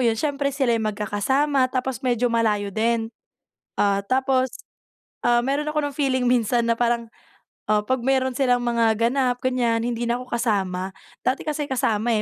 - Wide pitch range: No, narrow, 2.6 semitones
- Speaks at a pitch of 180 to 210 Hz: No, high, 240 Hz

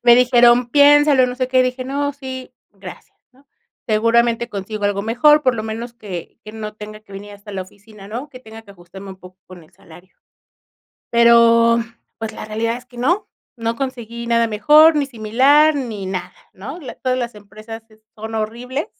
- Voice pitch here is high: Yes, high, 230 Hz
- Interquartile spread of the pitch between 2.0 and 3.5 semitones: Yes, average, 3.1 semitones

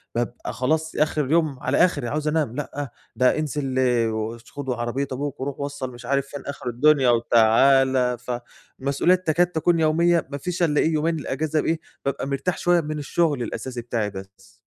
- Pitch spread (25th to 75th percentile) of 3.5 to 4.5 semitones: Yes, average, 4.0 semitones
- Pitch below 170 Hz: Yes, medium, 140 Hz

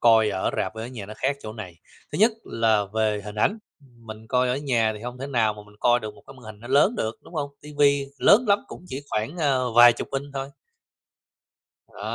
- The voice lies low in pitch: Yes, low, 120 Hz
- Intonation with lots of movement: No, average, 4.3 semitones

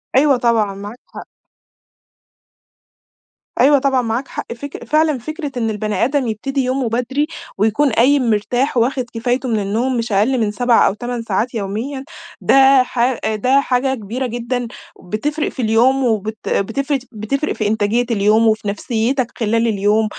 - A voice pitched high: Yes, high, 240 Hz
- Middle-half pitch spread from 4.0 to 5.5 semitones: No, average, 3.4 semitones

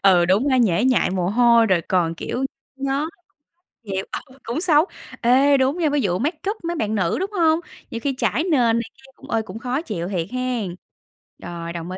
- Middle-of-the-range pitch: No, high, 245 Hz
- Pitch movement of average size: No, wide, 6.9 semitones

